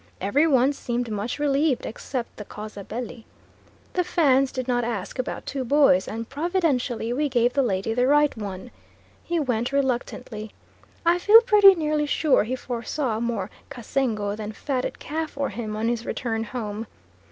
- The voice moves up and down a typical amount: Yes, average, 4.5 semitones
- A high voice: Yes, very high, 250 Hz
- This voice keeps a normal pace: Yes, average, 165 wpm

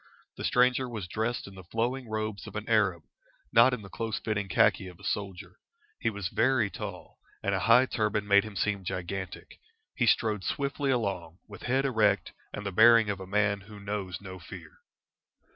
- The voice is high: No, low, 105 Hz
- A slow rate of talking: No, average, 195 wpm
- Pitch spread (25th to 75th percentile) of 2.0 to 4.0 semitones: Yes, average, 3.0 semitones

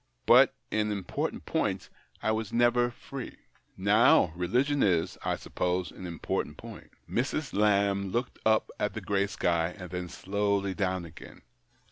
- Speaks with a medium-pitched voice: No, low, 100 Hz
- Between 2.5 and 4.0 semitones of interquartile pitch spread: Yes, average, 3.4 semitones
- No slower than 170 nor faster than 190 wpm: No, average, 145 wpm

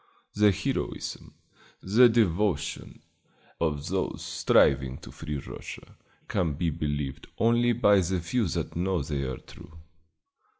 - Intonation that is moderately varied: No, wide, 5.9 semitones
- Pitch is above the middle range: No, very low, 85 Hz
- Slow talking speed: Yes, slow, 125 wpm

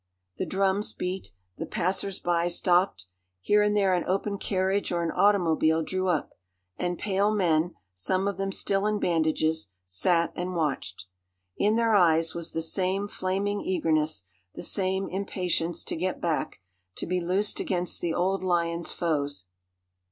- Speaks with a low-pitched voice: No, medium, 180 Hz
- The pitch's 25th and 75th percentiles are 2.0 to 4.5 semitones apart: Yes, average, 2.8 semitones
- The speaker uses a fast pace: No, average, 155 wpm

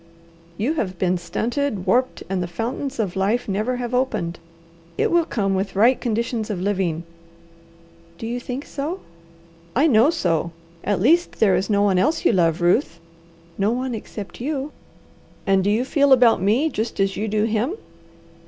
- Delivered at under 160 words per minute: No, average, 170 wpm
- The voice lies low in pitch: No, high, 220 Hz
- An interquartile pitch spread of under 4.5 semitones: No, average, 4.9 semitones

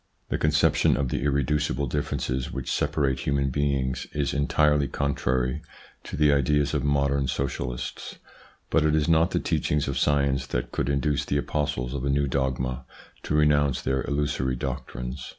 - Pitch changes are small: Yes, narrow, 2.0 semitones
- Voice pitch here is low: Yes, very low, 70 Hz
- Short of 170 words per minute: Yes, average, 160 wpm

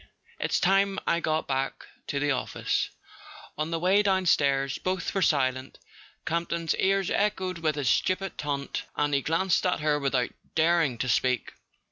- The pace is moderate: Yes, average, 160 wpm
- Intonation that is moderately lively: Yes, average, 5.0 semitones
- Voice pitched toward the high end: No, medium, 160 Hz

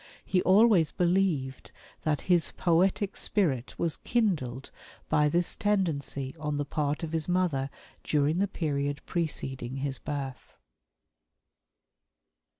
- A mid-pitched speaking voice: Yes, medium, 155 Hz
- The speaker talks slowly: Yes, slow, 115 wpm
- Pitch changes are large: No, average, 4.5 semitones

